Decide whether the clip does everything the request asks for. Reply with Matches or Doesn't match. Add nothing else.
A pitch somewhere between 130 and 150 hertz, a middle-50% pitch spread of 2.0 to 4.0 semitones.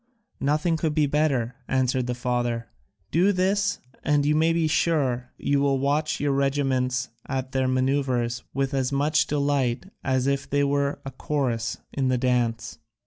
Matches